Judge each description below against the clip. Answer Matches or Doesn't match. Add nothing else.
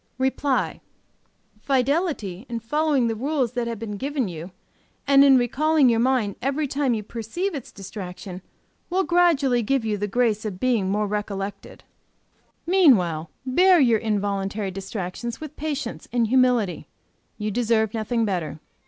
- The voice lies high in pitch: Matches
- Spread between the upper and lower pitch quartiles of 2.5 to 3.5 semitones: Doesn't match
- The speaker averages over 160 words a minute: Doesn't match